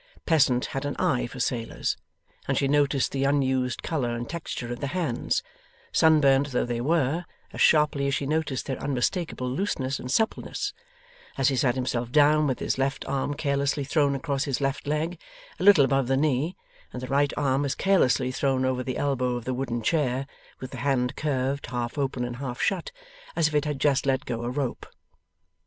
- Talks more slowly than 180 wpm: No, average, 195 wpm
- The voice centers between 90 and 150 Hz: Yes, low, 135 Hz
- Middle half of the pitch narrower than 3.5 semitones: Yes, narrow, 2.4 semitones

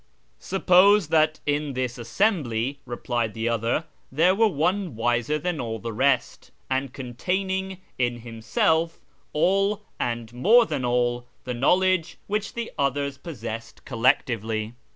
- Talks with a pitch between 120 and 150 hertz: Yes, medium, 140 Hz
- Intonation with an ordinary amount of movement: No, wide, 7.0 semitones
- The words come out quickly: No, slow, 135 wpm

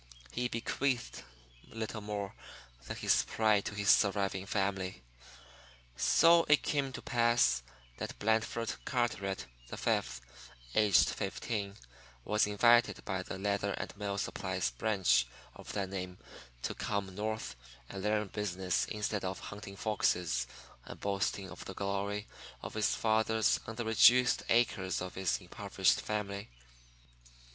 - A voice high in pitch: No, low, 105 Hz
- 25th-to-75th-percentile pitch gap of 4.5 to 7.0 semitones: No, narrow, 2.4 semitones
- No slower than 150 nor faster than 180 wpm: No, slow, 135 wpm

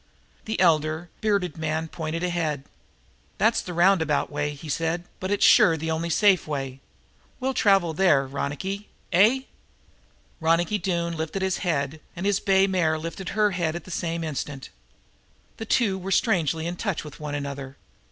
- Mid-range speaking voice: Yes, medium, 165 Hz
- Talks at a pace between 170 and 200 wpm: No, average, 160 wpm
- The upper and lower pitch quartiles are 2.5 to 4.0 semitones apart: Yes, average, 3.6 semitones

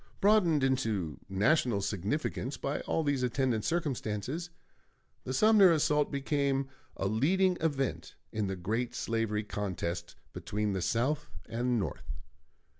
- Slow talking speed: Yes, slow, 120 wpm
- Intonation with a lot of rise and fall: Yes, wide, 6.1 semitones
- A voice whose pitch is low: Yes, low, 125 Hz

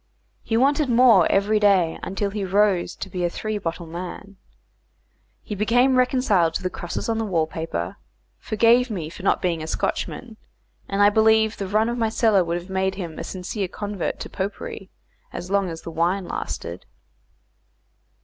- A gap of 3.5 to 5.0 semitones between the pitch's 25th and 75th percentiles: Yes, average, 3.8 semitones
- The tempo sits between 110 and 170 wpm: No, average, 180 wpm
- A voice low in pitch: No, high, 195 Hz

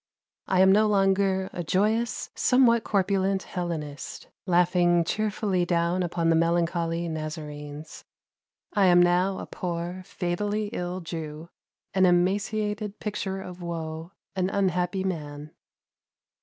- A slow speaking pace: Yes, slow, 115 wpm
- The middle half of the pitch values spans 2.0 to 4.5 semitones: Yes, narrow, 2.5 semitones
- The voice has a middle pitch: Yes, medium, 180 Hz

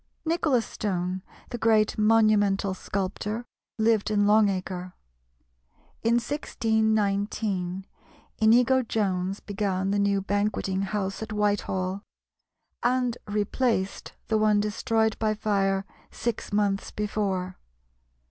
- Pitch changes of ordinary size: No, narrow, 2.1 semitones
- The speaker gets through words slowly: Yes, slow, 100 wpm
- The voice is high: Yes, high, 210 Hz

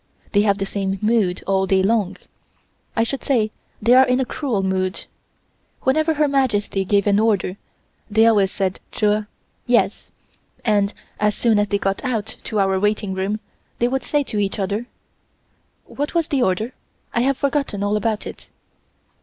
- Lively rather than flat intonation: No, average, 3.7 semitones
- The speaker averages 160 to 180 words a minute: Yes, average, 170 wpm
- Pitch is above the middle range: Yes, high, 210 Hz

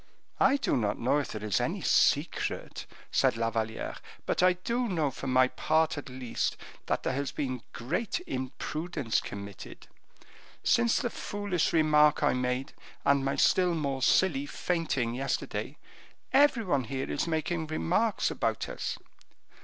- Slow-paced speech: No, average, 150 wpm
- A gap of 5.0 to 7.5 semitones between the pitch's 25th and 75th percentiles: Yes, wide, 5.6 semitones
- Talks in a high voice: No, medium, 145 Hz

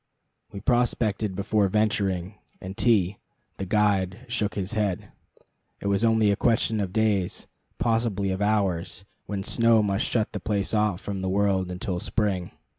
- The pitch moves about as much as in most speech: No, narrow, 2.3 semitones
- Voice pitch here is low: Yes, low, 100 Hz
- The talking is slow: No, average, 155 wpm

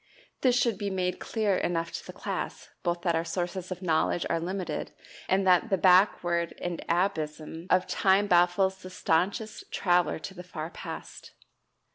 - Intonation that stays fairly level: Yes, narrow, 2.0 semitones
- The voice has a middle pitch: Yes, medium, 180 Hz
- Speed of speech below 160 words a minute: No, average, 165 wpm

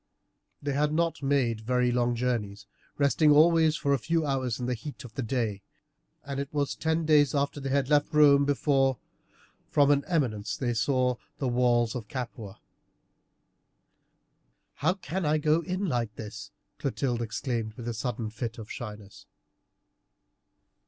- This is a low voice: Yes, low, 130 Hz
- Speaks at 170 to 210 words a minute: No, average, 155 wpm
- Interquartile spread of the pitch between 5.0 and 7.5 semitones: No, average, 3.7 semitones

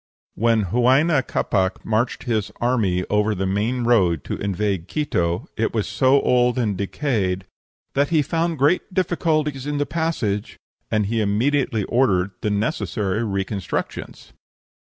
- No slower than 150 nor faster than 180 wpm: No, slow, 135 wpm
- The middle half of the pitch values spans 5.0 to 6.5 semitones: Yes, wide, 5.5 semitones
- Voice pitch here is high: No, low, 115 Hz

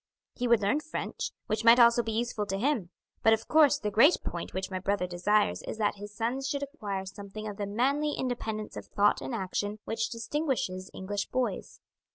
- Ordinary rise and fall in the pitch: Yes, average, 3.5 semitones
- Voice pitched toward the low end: No, high, 215 Hz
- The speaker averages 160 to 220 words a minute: Yes, average, 200 wpm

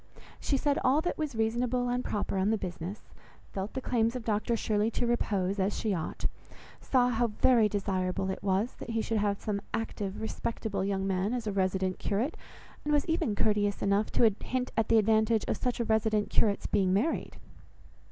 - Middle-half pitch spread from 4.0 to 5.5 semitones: No, average, 3.1 semitones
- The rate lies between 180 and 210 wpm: Yes, average, 190 wpm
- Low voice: No, high, 215 Hz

